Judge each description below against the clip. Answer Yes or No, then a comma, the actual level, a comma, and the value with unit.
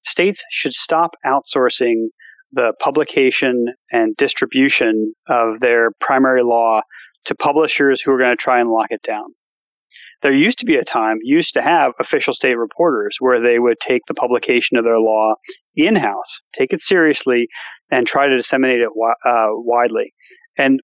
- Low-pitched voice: Yes, low, 130 Hz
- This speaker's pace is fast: No, average, 165 wpm